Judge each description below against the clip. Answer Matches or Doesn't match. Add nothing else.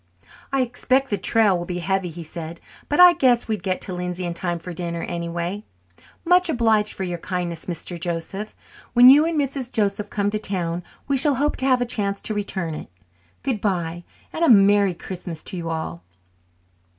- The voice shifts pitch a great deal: Matches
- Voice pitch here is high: Matches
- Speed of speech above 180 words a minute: Matches